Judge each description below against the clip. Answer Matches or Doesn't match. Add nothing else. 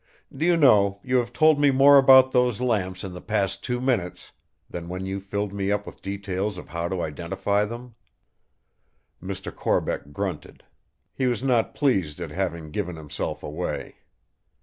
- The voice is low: Matches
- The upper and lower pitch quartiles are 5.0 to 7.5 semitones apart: Matches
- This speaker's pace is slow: Doesn't match